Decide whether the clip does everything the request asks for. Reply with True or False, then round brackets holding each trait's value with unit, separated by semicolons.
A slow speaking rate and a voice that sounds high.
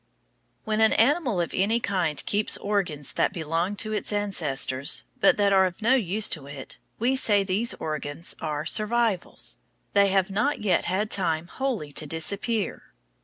False (165 wpm; 195 Hz)